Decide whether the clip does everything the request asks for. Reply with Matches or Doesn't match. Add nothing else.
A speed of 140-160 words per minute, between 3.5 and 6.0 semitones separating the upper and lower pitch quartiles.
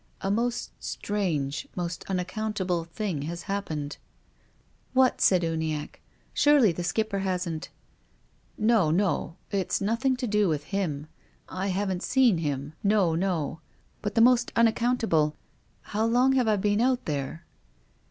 Matches